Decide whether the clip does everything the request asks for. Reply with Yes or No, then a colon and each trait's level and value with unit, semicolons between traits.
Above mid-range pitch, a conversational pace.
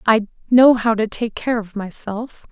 Yes: high, 225 Hz; average, 190 wpm